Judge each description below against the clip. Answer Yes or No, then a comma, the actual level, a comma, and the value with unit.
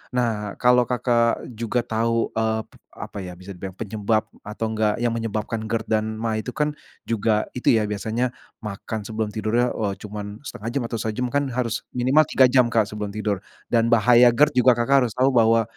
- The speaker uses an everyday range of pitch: No, narrow, 2.3 semitones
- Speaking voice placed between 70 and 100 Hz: No, low, 115 Hz